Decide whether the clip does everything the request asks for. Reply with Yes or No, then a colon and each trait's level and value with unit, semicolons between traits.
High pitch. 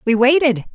Yes: very high, 255 Hz